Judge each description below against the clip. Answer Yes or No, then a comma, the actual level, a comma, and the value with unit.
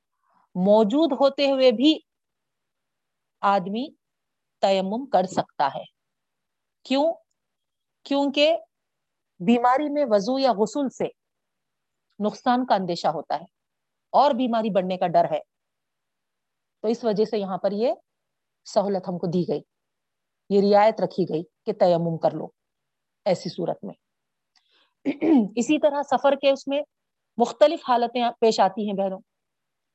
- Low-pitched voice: No, high, 230 Hz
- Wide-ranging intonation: Yes, wide, 6.0 semitones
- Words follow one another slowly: No, average, 125 wpm